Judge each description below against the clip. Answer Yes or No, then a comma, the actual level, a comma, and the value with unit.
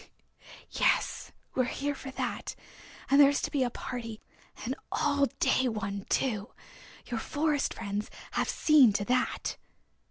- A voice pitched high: Yes, very high, 255 Hz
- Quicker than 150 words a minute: No, average, 145 wpm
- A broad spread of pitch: No, average, 4.4 semitones